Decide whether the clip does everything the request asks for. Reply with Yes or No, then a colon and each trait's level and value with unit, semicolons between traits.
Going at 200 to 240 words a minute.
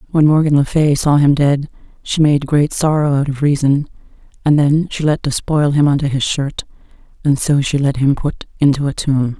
Yes: fast, 205 wpm